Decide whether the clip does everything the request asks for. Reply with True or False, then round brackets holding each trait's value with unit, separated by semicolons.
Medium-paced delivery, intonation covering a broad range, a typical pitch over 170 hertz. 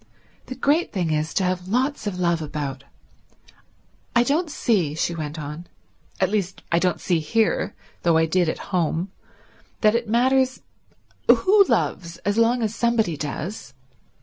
True (155 wpm; 6.5 semitones; 185 Hz)